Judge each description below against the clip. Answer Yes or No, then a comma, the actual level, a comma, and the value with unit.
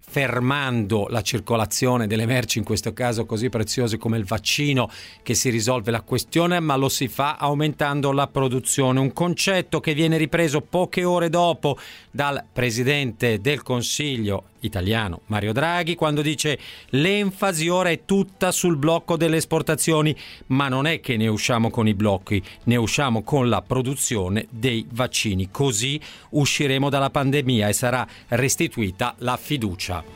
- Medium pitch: No, low, 130 Hz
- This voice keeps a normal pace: Yes, average, 150 wpm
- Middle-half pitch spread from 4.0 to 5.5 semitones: Yes, average, 5.0 semitones